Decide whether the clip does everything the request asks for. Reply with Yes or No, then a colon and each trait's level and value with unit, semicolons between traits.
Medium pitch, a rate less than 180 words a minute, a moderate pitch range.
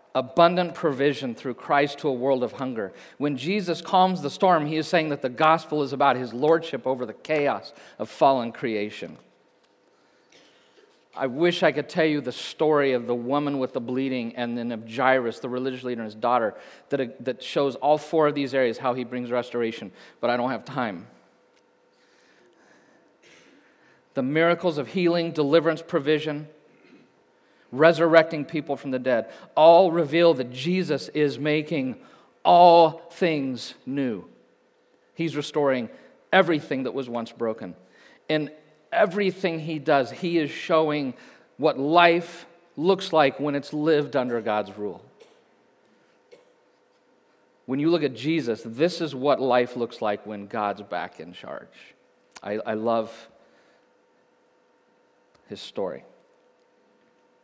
Yes: medium, 145 Hz; average, 140 wpm; average, 4.8 semitones